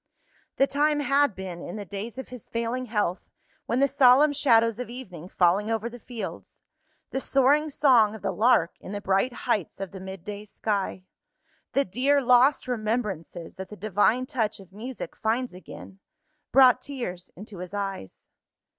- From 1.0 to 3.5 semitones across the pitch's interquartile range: No, average, 4.8 semitones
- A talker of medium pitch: No, high, 225 Hz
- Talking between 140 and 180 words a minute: Yes, average, 165 wpm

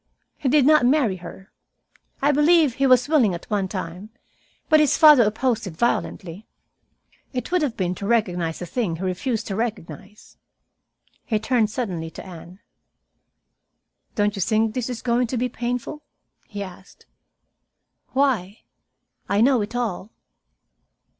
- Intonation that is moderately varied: Yes, average, 5.0 semitones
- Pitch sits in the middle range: No, high, 225 Hz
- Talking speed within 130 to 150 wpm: Yes, average, 145 wpm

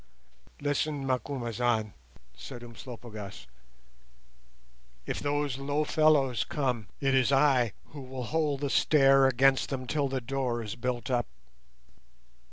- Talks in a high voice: No, low, 130 Hz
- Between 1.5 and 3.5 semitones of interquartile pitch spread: Yes, average, 2.9 semitones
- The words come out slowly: Yes, slow, 120 wpm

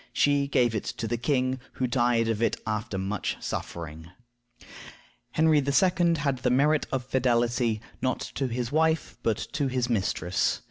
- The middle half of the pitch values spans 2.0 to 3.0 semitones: No, average, 3.7 semitones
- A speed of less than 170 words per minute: Yes, average, 155 wpm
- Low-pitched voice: Yes, low, 125 Hz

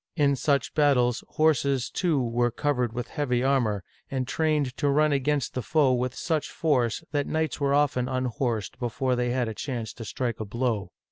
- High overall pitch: No, low, 130 Hz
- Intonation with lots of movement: No, average, 3.1 semitones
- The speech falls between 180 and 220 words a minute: Yes, average, 185 wpm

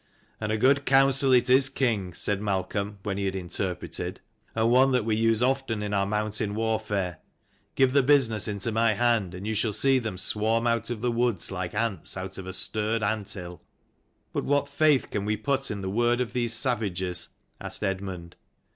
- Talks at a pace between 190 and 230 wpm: Yes, average, 200 wpm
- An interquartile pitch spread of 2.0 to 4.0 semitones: Yes, average, 3.7 semitones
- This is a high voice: No, low, 110 Hz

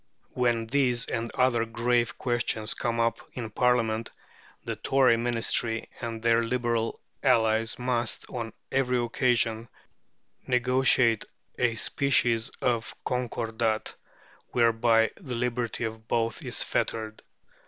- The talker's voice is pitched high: No, low, 115 Hz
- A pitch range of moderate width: No, narrow, 1.5 semitones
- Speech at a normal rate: No, slow, 110 wpm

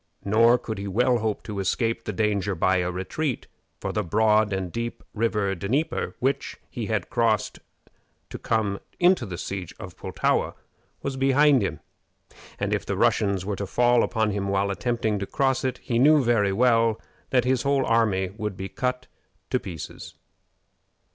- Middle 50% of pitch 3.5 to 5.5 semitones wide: Yes, average, 3.9 semitones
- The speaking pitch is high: No, low, 110 Hz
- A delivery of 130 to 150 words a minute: No, average, 170 wpm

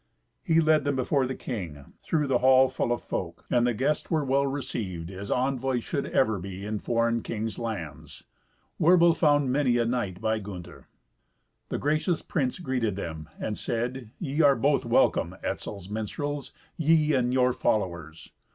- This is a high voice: No, low, 125 Hz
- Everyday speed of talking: Yes, average, 165 wpm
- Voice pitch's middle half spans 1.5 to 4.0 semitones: No, average, 5.3 semitones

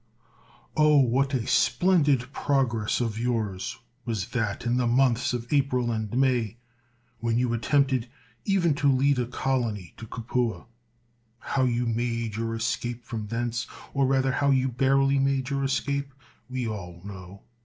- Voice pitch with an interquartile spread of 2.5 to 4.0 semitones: Yes, average, 2.9 semitones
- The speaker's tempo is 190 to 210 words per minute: No, average, 150 wpm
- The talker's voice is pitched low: Yes, low, 125 Hz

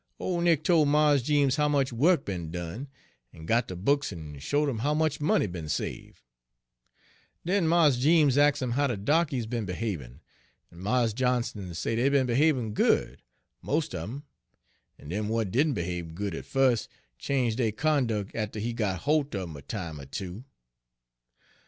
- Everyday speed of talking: Yes, average, 185 wpm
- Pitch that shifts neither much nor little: No, wide, 7.1 semitones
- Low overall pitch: Yes, low, 120 Hz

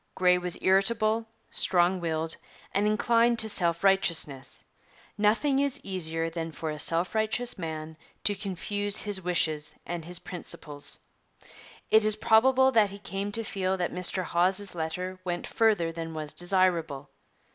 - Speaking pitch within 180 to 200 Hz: Yes, medium, 185 Hz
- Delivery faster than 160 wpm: No, average, 145 wpm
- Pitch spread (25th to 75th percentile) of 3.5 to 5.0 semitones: Yes, average, 4.2 semitones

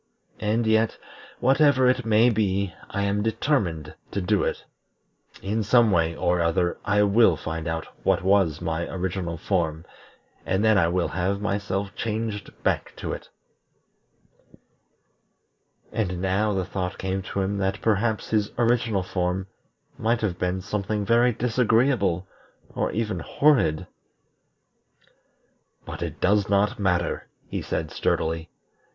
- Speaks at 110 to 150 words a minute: Yes, slow, 135 wpm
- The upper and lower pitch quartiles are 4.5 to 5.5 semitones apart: No, average, 3.4 semitones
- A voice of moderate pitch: No, low, 100 Hz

